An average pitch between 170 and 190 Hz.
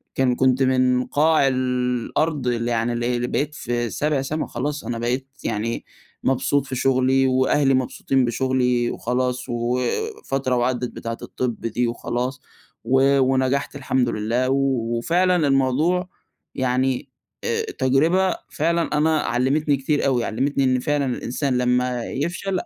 No: low, 130 Hz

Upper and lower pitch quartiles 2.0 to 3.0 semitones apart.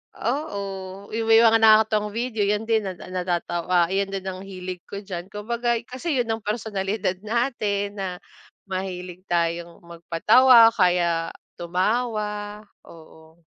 No: average, 3.6 semitones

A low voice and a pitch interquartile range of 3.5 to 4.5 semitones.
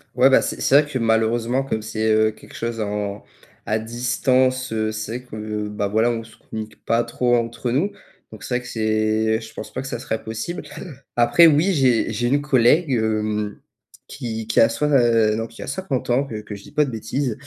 No: low, 115 Hz; average, 2.8 semitones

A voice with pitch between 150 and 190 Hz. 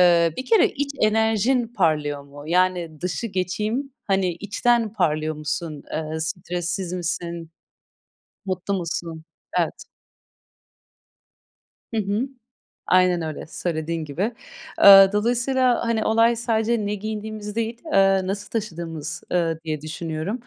Yes: medium, 185 Hz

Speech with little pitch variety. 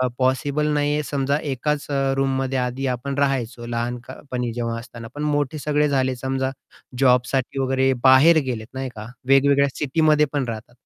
Yes: narrow, 2.3 semitones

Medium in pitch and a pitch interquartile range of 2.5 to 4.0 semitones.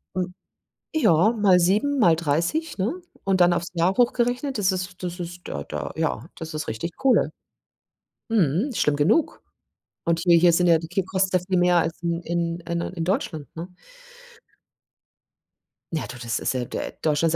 Yes: medium, 175 Hz; average, 2.8 semitones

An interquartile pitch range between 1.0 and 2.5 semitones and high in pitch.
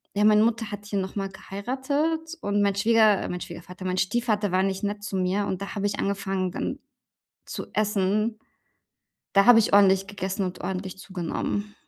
Yes: narrow, 1.9 semitones; high, 200 Hz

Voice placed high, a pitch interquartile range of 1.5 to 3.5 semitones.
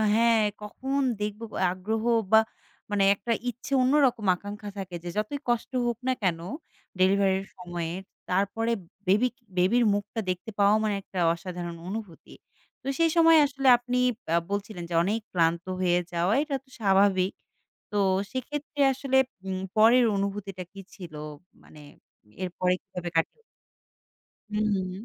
No: high, 205 Hz; average, 4.3 semitones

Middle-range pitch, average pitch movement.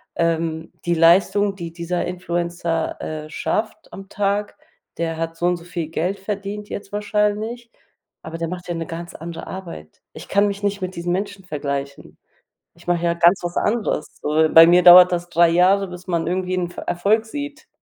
Yes: medium, 175 Hz; average, 3.0 semitones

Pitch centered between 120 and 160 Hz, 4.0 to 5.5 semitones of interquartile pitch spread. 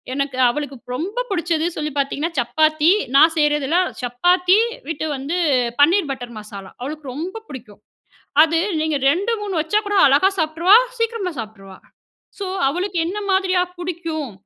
No: very high, 315 Hz; average, 4.7 semitones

